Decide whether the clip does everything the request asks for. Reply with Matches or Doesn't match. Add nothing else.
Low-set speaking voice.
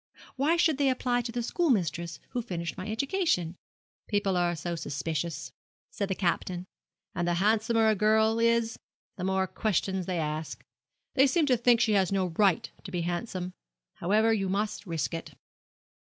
Doesn't match